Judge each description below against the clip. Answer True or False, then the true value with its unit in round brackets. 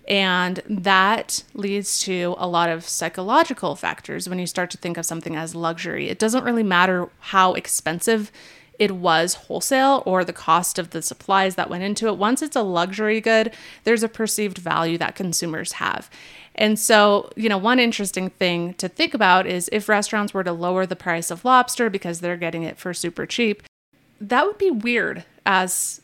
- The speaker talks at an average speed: True (185 wpm)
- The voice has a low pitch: False (185 Hz)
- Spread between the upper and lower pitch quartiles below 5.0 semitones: True (3.7 semitones)